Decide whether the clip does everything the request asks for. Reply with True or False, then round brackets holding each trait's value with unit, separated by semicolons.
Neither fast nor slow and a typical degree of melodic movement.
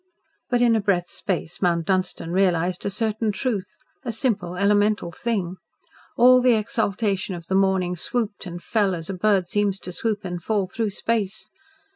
True (170 wpm; 3.4 semitones)